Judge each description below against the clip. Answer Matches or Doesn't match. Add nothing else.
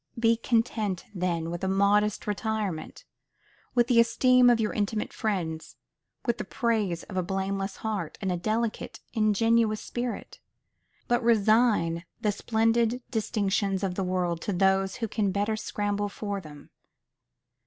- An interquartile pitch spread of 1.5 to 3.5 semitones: Matches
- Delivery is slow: Doesn't match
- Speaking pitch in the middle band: Doesn't match